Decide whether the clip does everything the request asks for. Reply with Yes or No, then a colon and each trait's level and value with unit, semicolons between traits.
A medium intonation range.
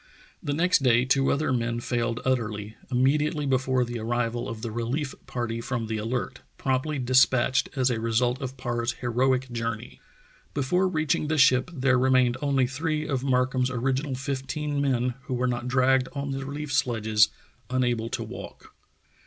No: narrow, 2.2 semitones